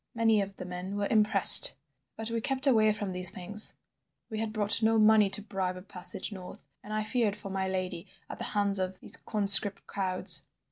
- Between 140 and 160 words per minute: No, average, 200 wpm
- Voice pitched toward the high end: Yes, high, 205 Hz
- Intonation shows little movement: Yes, narrow, 2.3 semitones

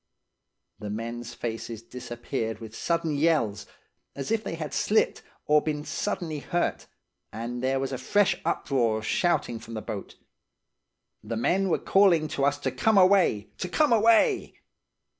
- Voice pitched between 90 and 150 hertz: Yes, medium, 140 Hz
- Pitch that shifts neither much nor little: No, wide, 7.2 semitones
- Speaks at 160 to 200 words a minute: No, average, 150 wpm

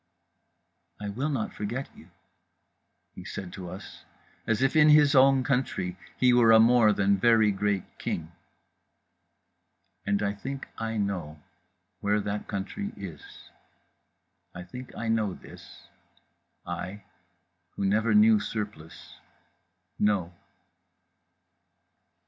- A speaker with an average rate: No, slow, 115 wpm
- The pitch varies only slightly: No, average, 3.6 semitones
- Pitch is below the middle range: Yes, low, 105 Hz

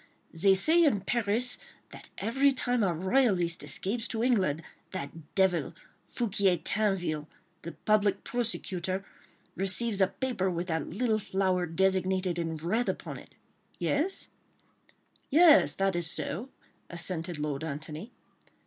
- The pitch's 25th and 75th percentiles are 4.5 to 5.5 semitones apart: Yes, average, 5.1 semitones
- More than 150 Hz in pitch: Yes, high, 190 Hz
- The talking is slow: Yes, slow, 125 wpm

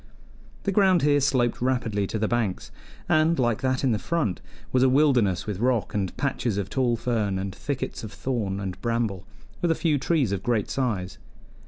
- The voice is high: No, low, 120 Hz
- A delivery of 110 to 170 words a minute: No, average, 190 wpm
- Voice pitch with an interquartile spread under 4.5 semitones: No, average, 4.9 semitones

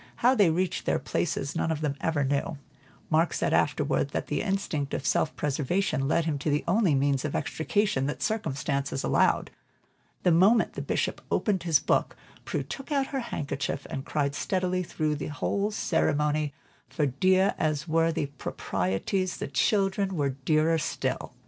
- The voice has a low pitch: No, medium, 155 Hz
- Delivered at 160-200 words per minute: Yes, average, 170 wpm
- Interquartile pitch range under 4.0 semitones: No, average, 4.7 semitones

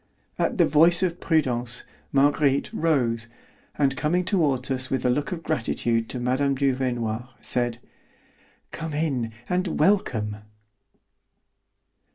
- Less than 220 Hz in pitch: Yes, low, 135 Hz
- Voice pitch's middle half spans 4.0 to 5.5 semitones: Yes, average, 4.4 semitones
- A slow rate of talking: Yes, slow, 120 wpm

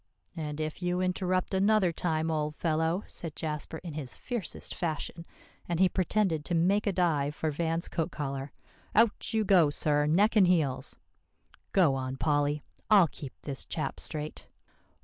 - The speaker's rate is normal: Yes, average, 160 wpm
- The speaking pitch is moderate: Yes, medium, 165 Hz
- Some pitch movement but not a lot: Yes, average, 3.6 semitones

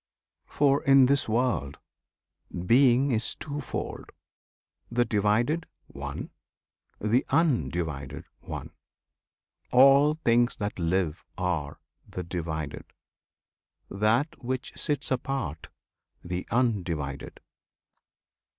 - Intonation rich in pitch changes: Yes, wide, 7.6 semitones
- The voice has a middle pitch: No, low, 115 Hz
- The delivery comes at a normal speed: No, slow, 85 wpm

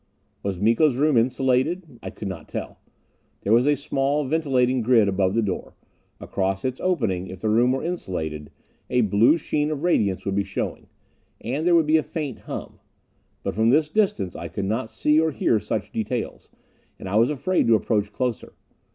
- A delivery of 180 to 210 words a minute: Yes, average, 185 wpm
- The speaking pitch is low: Yes, low, 120 Hz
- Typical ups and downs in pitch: No, wide, 6.6 semitones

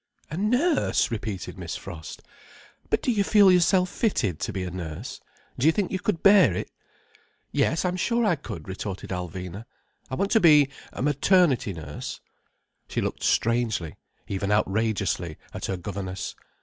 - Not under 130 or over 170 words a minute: Yes, average, 160 wpm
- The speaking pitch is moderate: No, low, 115 Hz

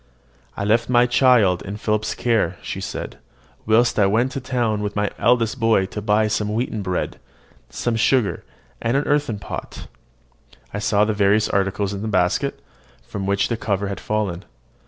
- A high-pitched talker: No, low, 105 Hz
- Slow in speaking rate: No, average, 180 wpm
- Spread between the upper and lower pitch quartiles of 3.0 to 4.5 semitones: No, narrow, 2.6 semitones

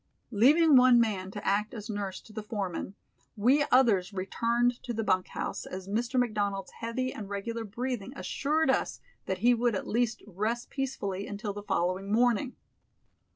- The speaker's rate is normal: Yes, average, 165 wpm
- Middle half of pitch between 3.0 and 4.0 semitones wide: Yes, average, 3.5 semitones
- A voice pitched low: No, high, 220 Hz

